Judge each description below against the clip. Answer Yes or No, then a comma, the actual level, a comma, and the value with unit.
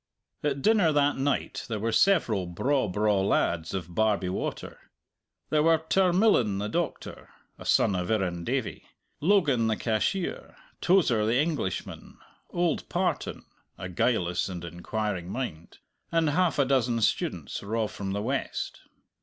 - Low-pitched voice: Yes, low, 115 Hz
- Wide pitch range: Yes, wide, 7.5 semitones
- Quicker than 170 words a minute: No, slow, 135 wpm